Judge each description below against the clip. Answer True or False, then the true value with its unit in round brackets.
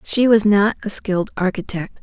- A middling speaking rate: True (180 wpm)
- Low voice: False (205 Hz)